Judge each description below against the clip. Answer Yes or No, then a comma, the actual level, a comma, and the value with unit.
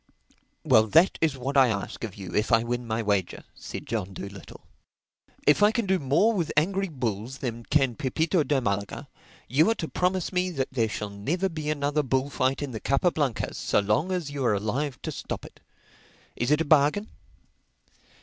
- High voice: No, low, 135 Hz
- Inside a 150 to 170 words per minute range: No, average, 190 wpm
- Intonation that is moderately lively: No, wide, 6.0 semitones